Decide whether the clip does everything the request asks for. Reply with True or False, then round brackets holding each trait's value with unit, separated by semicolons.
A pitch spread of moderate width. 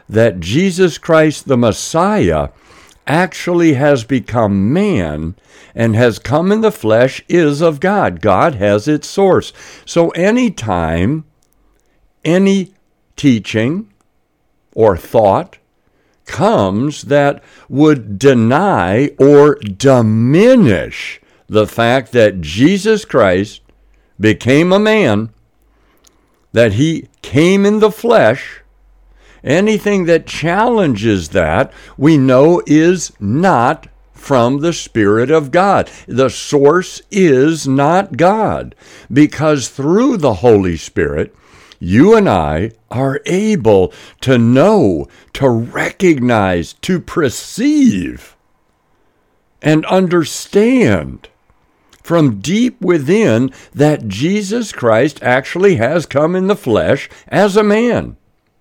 False (8.2 semitones)